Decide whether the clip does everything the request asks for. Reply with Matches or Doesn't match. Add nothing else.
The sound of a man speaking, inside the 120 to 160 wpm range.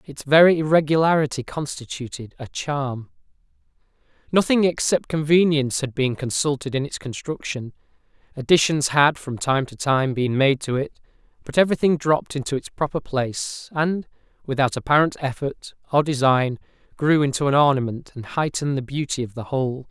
Matches